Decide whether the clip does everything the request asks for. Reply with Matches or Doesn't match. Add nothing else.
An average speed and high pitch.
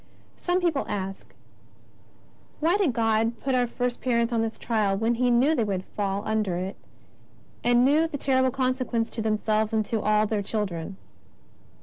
Matches